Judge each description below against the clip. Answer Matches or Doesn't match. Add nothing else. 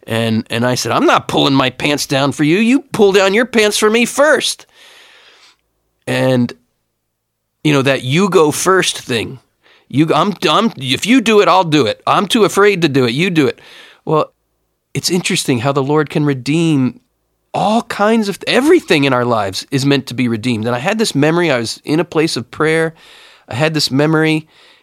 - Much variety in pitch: Matches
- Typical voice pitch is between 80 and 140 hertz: Doesn't match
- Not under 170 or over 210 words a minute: Matches